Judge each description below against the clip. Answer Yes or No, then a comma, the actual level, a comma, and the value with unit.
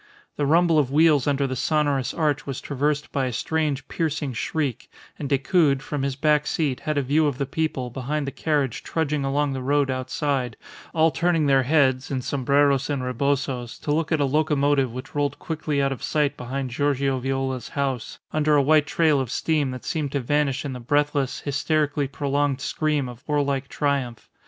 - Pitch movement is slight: Yes, narrow, 2.1 semitones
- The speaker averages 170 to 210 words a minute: Yes, average, 190 wpm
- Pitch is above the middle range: No, medium, 140 Hz